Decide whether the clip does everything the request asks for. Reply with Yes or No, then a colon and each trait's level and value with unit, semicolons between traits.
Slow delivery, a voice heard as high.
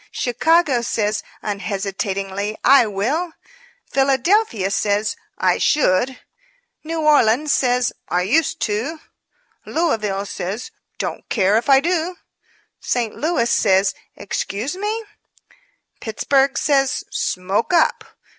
Yes: slow, 105 wpm; high, 240 Hz